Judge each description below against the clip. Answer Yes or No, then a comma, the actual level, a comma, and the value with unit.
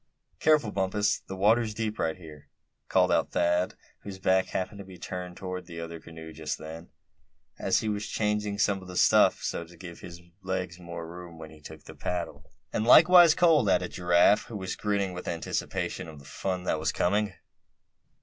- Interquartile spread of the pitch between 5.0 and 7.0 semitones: No, average, 3.4 semitones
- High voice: No, very low, 90 Hz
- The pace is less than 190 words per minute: No, average, 195 wpm